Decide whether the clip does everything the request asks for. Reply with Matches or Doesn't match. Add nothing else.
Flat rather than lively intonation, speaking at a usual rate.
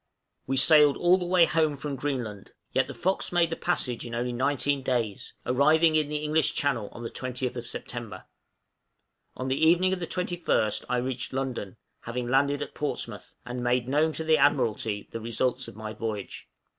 Doesn't match